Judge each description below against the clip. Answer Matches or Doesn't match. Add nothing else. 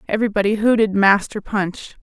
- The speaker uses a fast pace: Doesn't match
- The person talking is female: Matches